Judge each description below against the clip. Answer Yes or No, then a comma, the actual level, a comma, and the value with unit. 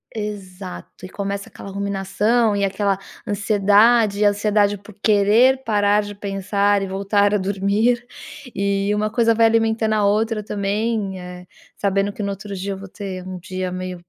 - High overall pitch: Yes, high, 200 Hz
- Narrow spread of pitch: Yes, narrow, 1.4 semitones